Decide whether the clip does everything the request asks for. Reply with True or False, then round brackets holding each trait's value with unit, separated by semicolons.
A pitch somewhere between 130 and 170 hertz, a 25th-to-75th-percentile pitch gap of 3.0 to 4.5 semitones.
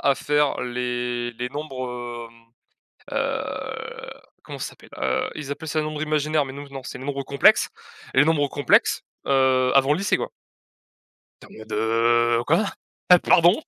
True (135 Hz; 3.3 semitones)